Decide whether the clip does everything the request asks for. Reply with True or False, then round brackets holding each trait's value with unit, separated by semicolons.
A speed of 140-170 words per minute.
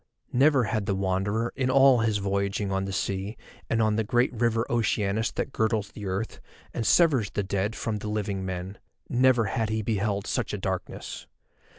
False (180 wpm)